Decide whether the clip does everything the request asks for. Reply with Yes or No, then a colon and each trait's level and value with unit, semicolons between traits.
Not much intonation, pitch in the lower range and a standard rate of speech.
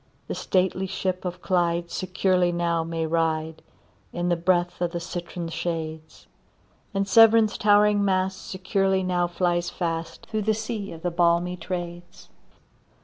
No: narrow, 1.9 semitones; medium, 175 Hz; average, 145 wpm